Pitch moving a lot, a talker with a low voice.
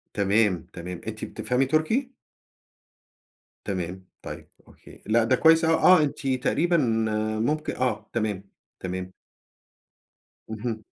Yes: wide, 7.3 semitones; low, 115 Hz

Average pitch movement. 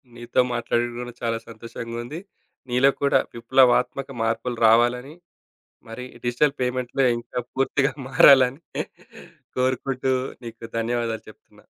No: narrow, 2.1 semitones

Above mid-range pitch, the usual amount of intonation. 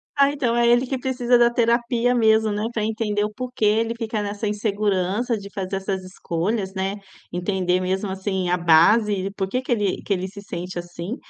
Yes: high, 210 Hz; average, 3.7 semitones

